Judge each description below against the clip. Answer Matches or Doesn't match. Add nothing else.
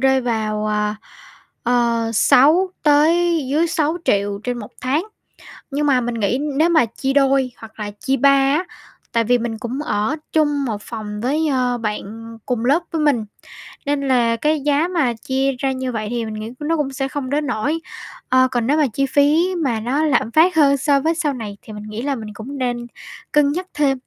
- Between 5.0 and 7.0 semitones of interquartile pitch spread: Doesn't match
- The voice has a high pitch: Matches